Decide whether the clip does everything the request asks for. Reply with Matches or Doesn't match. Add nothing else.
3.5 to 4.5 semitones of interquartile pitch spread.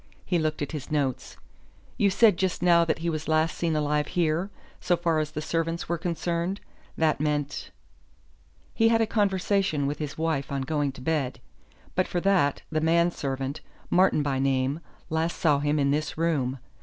Doesn't match